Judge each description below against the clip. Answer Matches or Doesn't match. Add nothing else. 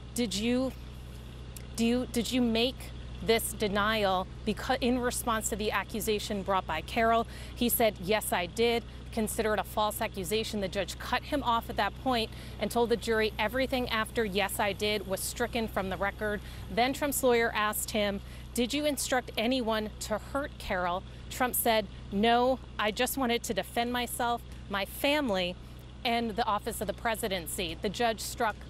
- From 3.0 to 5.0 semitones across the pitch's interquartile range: Doesn't match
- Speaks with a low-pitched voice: Doesn't match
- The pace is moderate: Matches